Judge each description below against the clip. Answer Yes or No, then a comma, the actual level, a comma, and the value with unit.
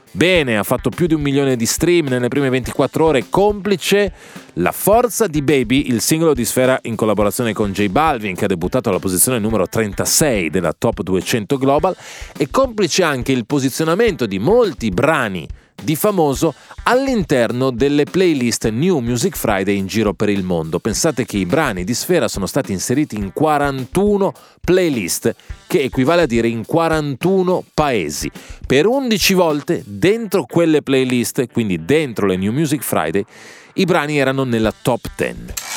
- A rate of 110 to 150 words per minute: No, average, 160 wpm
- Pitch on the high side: No, low, 135 Hz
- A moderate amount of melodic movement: No, wide, 6.9 semitones